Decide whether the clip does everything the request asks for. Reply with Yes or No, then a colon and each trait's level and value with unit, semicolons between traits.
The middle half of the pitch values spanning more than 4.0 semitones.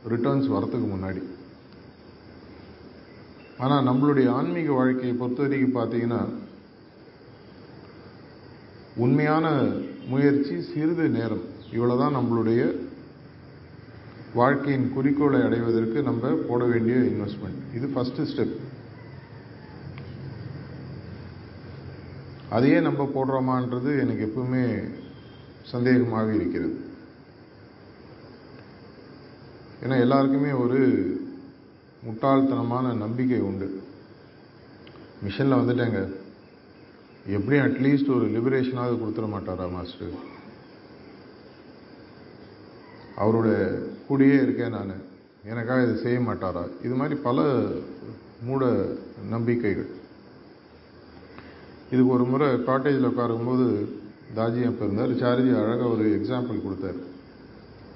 No: average, 3.3 semitones